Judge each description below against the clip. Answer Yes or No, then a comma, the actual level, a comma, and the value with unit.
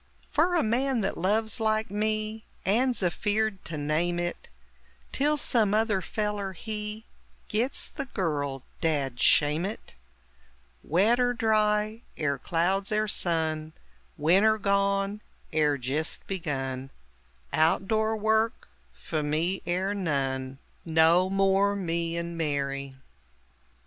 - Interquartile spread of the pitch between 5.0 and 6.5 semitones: Yes, wide, 5.4 semitones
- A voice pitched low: No, high, 195 Hz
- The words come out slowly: Yes, slow, 120 wpm